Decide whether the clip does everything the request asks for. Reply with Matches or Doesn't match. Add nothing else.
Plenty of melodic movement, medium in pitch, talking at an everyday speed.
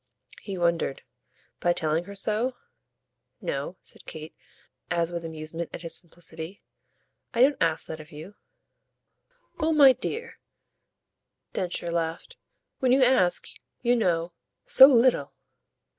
Doesn't match